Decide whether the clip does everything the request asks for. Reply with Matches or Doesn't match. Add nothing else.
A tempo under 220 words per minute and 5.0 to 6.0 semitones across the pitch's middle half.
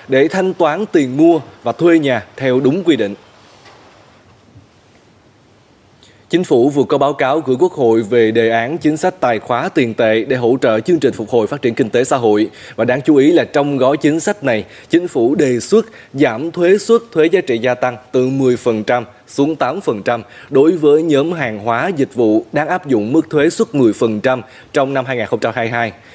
Matches